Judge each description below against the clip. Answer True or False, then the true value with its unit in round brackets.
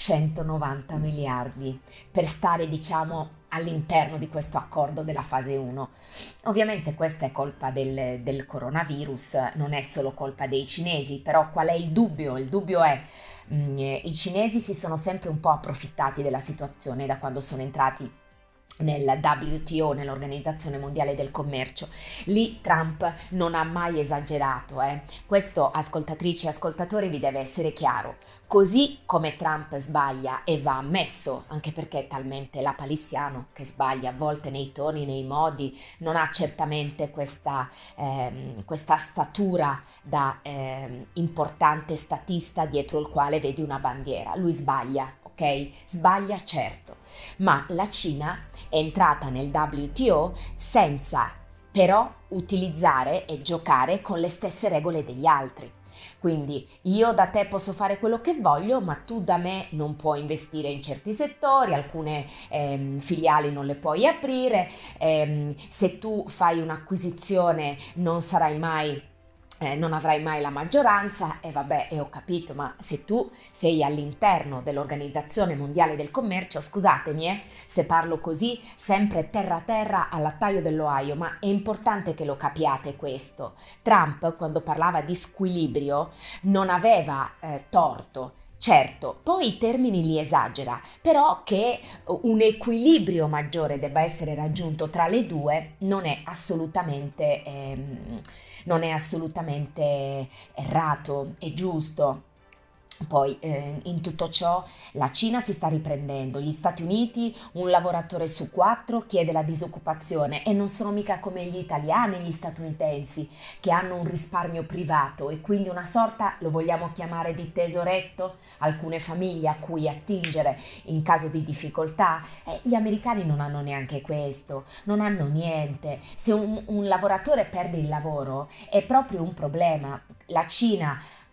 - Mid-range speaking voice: True (155 Hz)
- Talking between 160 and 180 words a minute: False (145 wpm)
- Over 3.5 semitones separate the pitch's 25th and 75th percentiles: True (3.9 semitones)